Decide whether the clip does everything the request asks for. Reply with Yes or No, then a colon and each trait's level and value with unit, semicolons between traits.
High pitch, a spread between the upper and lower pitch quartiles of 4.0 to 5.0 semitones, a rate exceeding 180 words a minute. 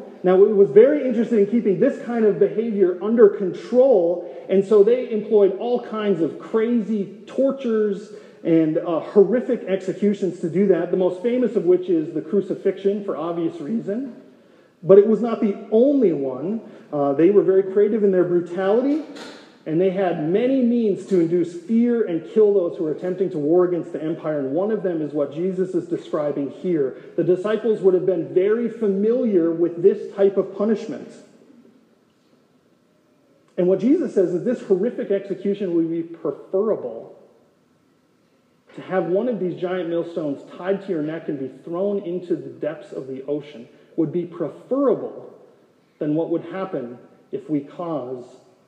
No: high, 195 Hz; average, 4.3 semitones; average, 170 wpm